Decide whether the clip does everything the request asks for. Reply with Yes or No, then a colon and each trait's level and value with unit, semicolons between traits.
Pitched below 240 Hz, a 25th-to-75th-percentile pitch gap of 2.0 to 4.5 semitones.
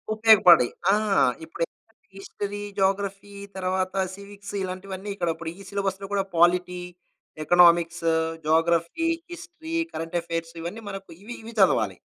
Yes: high, 190 Hz; average, 2.9 semitones